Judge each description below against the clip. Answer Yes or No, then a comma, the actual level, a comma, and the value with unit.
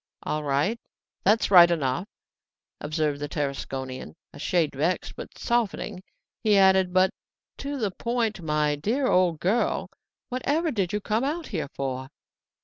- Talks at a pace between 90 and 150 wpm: Yes, average, 145 wpm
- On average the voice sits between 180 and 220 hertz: Yes, medium, 185 Hz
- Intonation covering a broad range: Yes, wide, 7.0 semitones